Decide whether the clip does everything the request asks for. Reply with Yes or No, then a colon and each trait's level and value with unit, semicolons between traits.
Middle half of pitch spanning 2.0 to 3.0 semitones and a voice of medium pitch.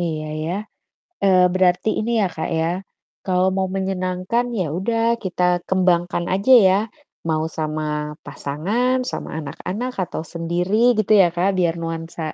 Yes: narrow, 2.6 semitones; medium, 180 Hz